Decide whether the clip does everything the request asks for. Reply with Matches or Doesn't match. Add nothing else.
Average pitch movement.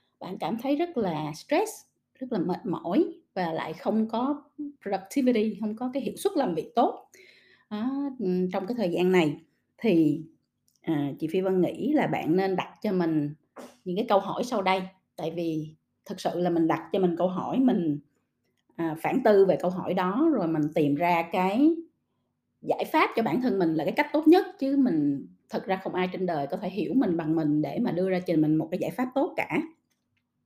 Doesn't match